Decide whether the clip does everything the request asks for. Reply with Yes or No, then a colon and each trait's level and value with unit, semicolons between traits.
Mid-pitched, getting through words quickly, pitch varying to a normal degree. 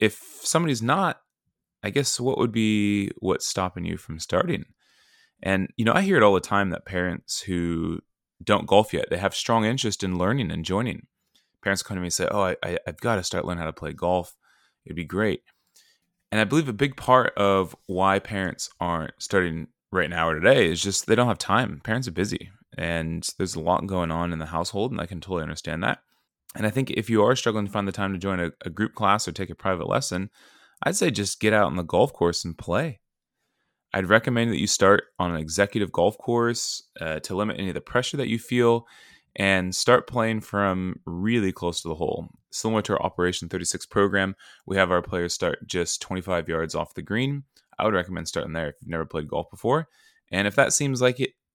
No: very low, 95 Hz; fast, 225 wpm; average, 4.0 semitones